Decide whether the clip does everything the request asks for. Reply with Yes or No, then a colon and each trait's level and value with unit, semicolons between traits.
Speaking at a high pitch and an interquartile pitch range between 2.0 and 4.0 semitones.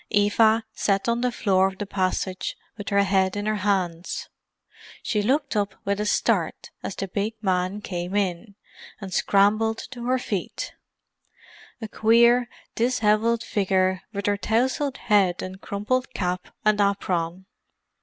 Yes: high, 205 Hz; average, 2.8 semitones